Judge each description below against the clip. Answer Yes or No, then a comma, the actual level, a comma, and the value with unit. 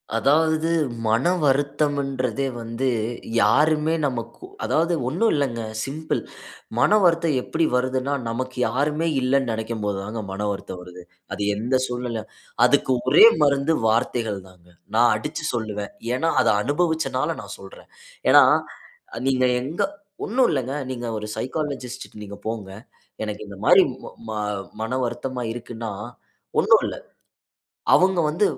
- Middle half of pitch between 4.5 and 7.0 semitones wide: Yes, average, 4.9 semitones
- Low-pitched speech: Yes, low, 130 Hz